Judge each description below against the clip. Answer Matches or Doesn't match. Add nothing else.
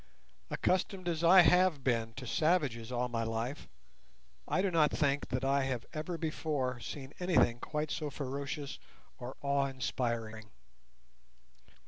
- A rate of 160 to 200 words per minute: Doesn't match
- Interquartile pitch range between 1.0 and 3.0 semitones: Doesn't match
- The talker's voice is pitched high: Doesn't match